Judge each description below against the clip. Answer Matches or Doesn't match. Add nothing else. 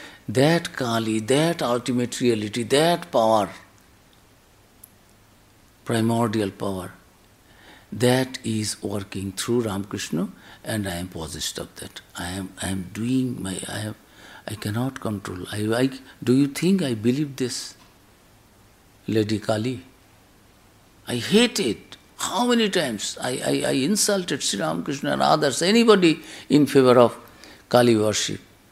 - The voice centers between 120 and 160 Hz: Doesn't match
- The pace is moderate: Doesn't match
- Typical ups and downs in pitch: Matches